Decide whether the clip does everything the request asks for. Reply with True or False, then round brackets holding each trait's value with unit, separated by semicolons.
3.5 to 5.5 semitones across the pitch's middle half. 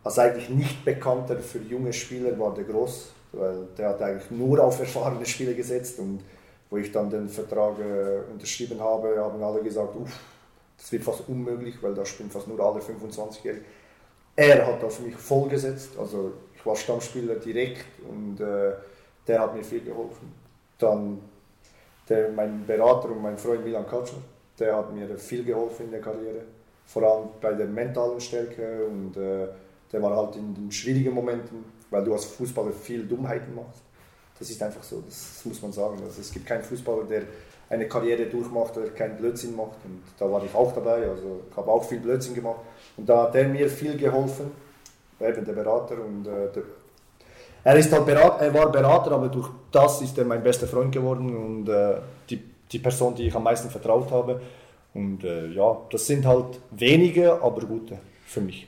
False (2.9 semitones)